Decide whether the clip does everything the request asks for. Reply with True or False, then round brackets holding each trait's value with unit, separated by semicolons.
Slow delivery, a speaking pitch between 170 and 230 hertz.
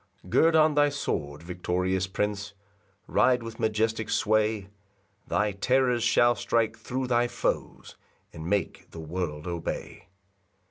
False (130 wpm; 110 Hz)